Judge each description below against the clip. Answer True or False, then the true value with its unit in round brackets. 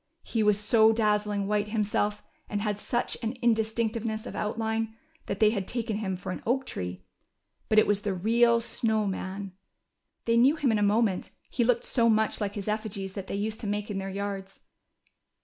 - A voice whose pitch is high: True (215 Hz)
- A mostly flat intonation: True (1.9 semitones)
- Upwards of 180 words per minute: True (200 wpm)